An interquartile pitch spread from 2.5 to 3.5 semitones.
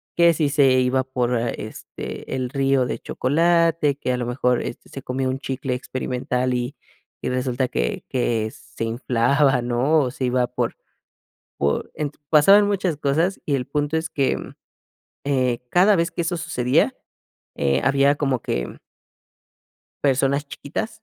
Yes: average, 3.0 semitones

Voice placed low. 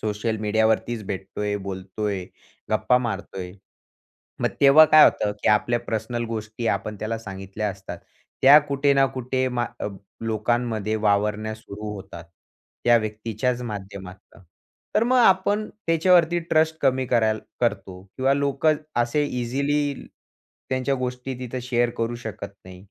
Yes: low, 115 Hz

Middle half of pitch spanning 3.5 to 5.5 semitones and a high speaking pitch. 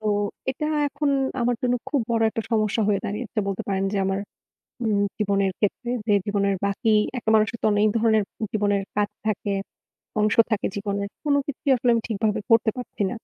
No: narrow, 2.6 semitones; high, 215 Hz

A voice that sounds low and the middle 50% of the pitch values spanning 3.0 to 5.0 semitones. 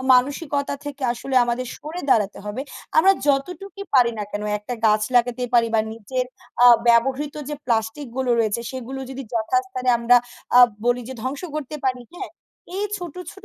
No: very high, 255 Hz; average, 3.3 semitones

